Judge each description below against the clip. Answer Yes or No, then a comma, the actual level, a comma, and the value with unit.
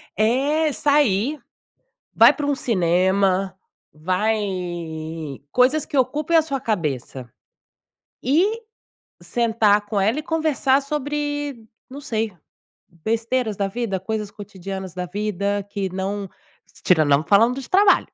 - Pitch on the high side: Yes, high, 220 Hz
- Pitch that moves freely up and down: Yes, wide, 6.4 semitones